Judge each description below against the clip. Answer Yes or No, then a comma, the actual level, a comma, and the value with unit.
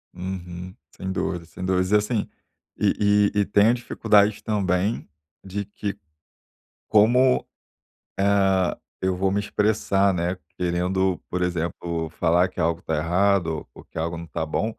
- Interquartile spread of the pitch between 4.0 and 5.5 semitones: No, average, 2.7 semitones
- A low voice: Yes, very low, 95 Hz